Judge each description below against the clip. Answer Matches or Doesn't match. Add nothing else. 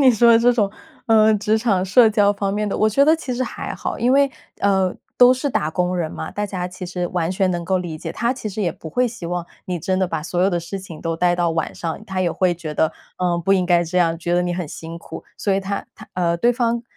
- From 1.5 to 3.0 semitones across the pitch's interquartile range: Doesn't match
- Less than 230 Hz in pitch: Matches